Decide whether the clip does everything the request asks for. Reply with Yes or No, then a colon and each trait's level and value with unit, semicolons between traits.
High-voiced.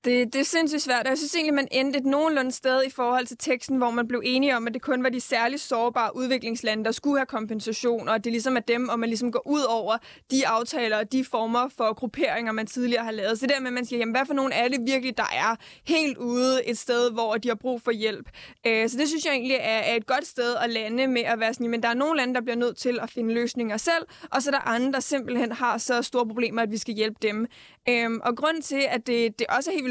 Yes: high, 245 Hz